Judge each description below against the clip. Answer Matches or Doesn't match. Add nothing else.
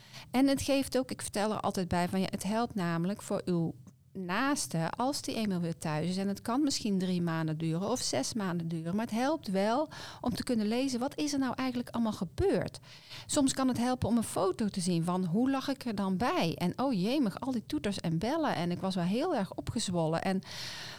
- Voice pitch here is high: Matches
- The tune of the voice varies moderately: Doesn't match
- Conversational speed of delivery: Doesn't match